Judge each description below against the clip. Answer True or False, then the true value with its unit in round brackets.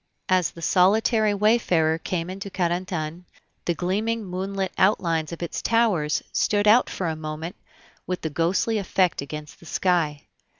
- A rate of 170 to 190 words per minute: False (140 wpm)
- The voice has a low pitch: False (180 Hz)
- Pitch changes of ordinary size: True (3.3 semitones)